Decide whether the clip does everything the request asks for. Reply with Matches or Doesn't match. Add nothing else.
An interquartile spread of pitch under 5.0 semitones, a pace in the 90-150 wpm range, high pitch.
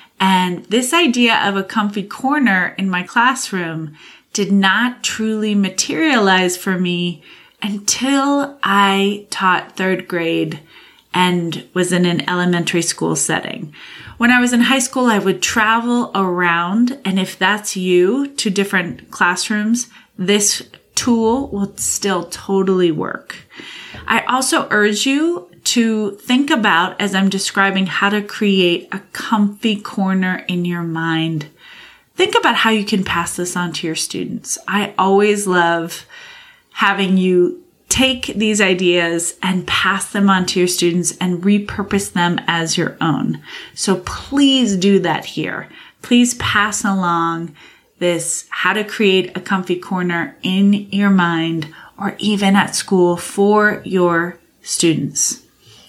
Matches